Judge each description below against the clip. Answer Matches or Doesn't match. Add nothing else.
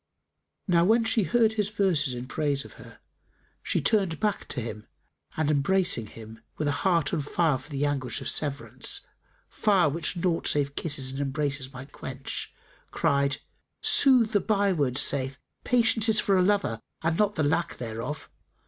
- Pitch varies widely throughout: Matches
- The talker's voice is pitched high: Doesn't match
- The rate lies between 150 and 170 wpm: Matches